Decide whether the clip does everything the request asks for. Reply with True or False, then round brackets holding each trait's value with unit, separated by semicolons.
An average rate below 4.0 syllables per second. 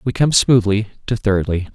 False (4.8 syllables/s)